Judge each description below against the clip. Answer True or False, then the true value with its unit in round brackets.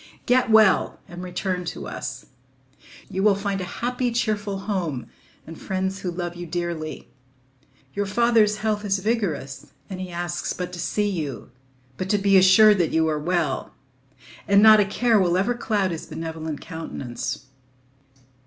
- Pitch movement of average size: True (3.4 semitones)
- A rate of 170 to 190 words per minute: False (155 wpm)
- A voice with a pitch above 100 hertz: True (190 Hz)